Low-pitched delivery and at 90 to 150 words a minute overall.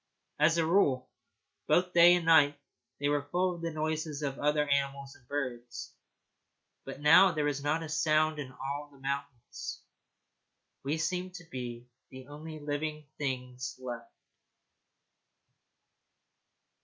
No: medium, 145 Hz; slow, 135 wpm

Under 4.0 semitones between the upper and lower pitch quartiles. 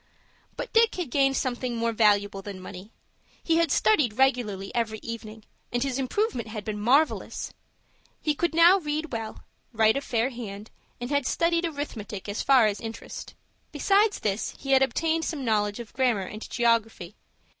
No: average, 5.0 semitones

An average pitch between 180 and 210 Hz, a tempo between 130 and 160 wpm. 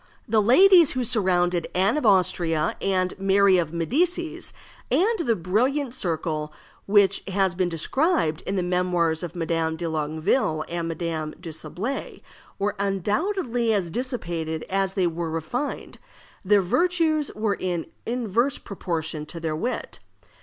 Yes: medium, 185 Hz; average, 140 wpm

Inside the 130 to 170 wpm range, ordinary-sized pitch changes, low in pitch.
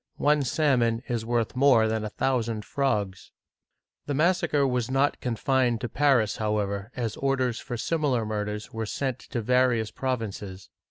Yes: average, 155 wpm; average, 3.5 semitones; low, 120 Hz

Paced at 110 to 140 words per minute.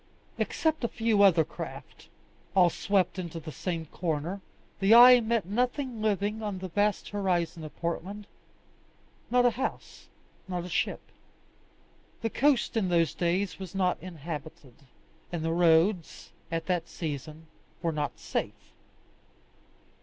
Yes: slow, 135 wpm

